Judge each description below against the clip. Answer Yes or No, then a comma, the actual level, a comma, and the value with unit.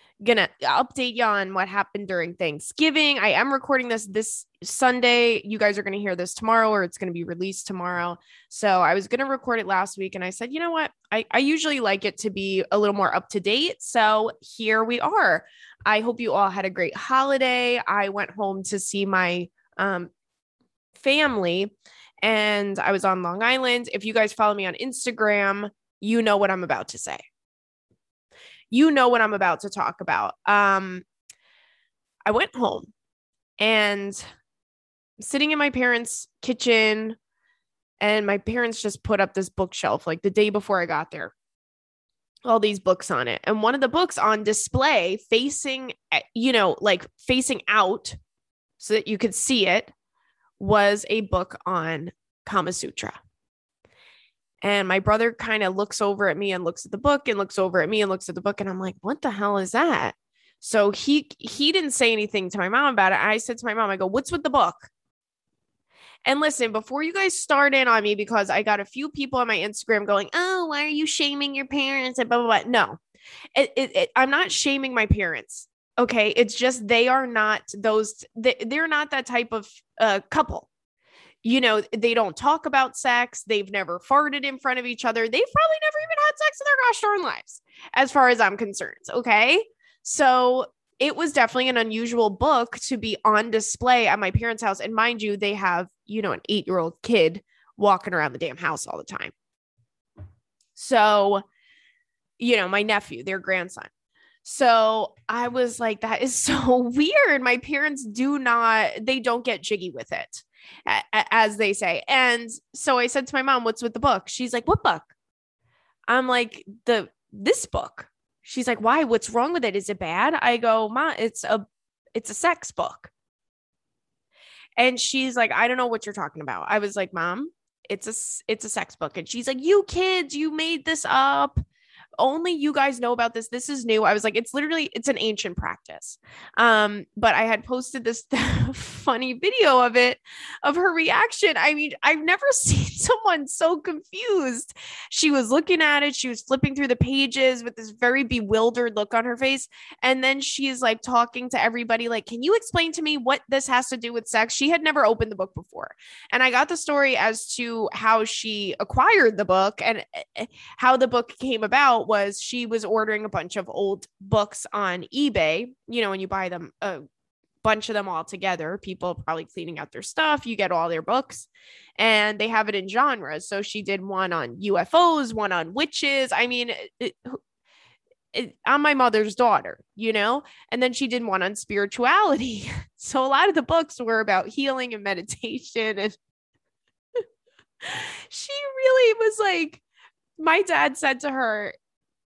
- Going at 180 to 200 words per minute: Yes, average, 190 wpm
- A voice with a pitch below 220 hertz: No, high, 230 Hz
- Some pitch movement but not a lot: Yes, average, 4.9 semitones